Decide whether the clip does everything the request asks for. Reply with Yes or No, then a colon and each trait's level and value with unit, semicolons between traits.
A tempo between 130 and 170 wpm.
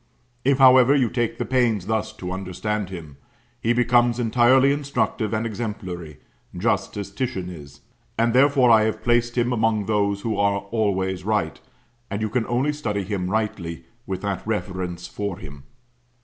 Yes: average, 160 wpm